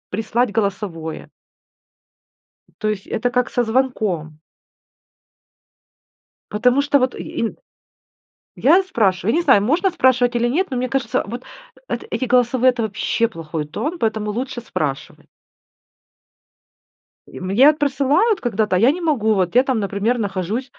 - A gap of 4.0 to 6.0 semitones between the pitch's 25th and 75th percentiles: Yes, average, 4.3 semitones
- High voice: Yes, high, 235 Hz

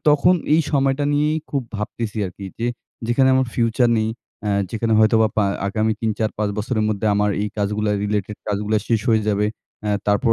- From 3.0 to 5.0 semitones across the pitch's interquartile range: No, narrow, 2.6 semitones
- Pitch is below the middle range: Yes, low, 110 Hz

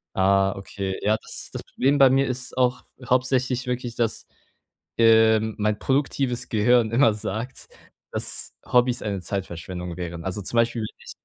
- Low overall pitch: Yes, low, 115 Hz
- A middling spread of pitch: Yes, average, 4.2 semitones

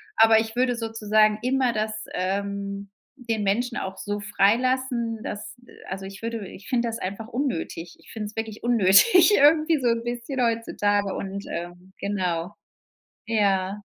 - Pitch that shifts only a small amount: No, average, 3.0 semitones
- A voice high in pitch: Yes, high, 215 Hz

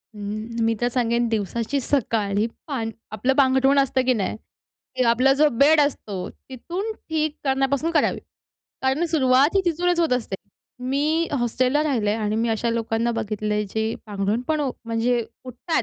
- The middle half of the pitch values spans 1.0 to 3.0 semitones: No, average, 4.1 semitones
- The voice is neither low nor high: No, very high, 250 Hz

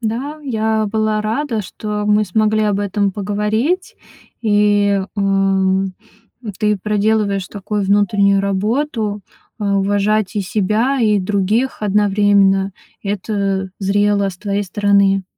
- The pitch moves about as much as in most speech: No, narrow, 1.5 semitones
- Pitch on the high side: Yes, high, 205 Hz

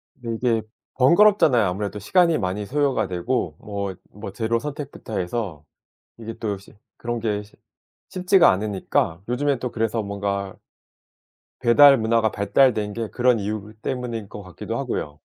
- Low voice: Yes, low, 110 Hz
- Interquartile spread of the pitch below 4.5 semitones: Yes, average, 3.8 semitones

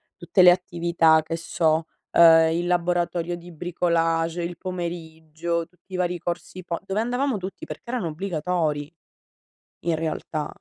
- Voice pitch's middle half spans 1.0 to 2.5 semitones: Yes, narrow, 1.6 semitones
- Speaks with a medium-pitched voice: Yes, medium, 170 Hz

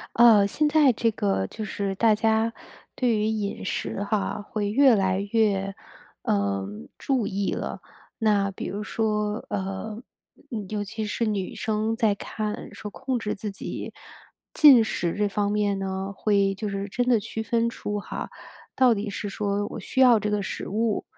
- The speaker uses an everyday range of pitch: No, narrow, 2.0 semitones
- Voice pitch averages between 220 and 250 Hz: No, high, 210 Hz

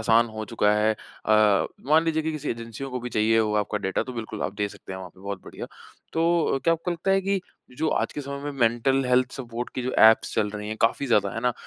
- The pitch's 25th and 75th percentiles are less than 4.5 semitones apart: No, average, 4.8 semitones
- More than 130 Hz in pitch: No, low, 115 Hz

